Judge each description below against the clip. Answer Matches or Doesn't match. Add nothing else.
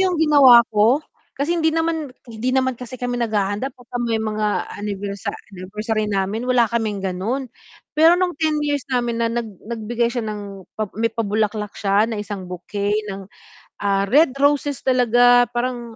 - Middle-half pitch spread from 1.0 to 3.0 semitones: Doesn't match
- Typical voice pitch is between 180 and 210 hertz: Doesn't match